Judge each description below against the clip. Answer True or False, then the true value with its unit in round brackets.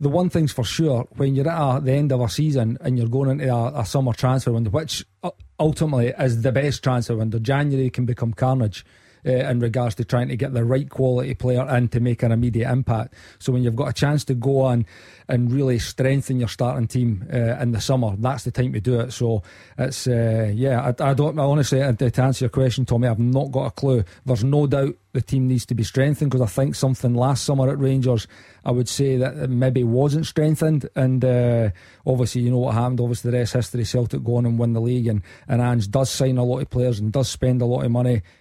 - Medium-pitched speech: False (125 Hz)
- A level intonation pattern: True (2.0 semitones)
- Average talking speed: False (240 wpm)